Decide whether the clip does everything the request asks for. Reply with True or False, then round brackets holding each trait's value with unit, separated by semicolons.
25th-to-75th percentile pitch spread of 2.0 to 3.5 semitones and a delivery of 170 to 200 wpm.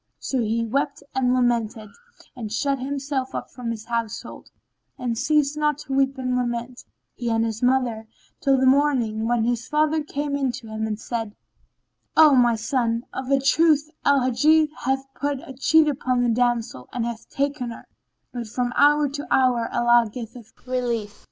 True (3.2 semitones; 175 wpm)